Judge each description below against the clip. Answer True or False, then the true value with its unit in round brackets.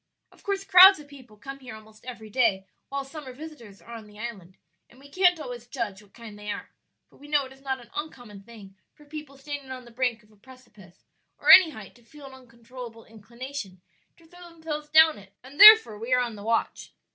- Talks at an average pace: False (225 wpm)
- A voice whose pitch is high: True (255 Hz)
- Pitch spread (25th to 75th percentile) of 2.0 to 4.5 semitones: False (5.0 semitones)